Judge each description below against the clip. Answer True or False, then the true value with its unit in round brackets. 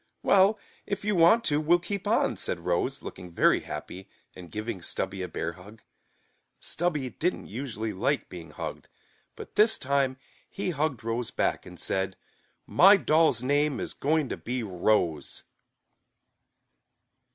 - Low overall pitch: True (130 Hz)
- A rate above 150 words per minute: False (145 wpm)